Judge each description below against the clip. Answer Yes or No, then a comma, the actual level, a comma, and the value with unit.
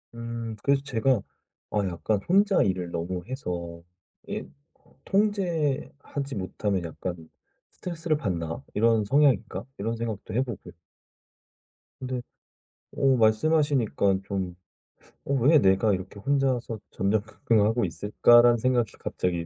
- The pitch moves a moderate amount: No, wide, 5.9 semitones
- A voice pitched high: No, low, 115 Hz